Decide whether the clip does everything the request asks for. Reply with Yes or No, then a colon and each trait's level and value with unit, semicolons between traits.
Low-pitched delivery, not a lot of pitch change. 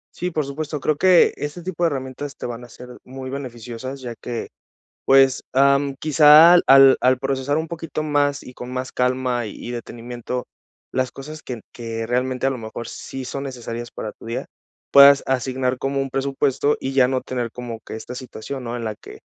Yes: low, 130 Hz; narrow, 2.3 semitones